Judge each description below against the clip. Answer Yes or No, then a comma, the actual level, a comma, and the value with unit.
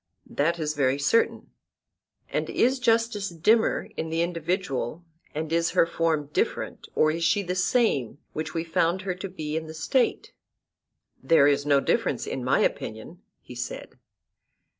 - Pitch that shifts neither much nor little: Yes, average, 3.5 semitones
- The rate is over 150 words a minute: Yes, average, 160 wpm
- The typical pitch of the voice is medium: Yes, medium, 165 Hz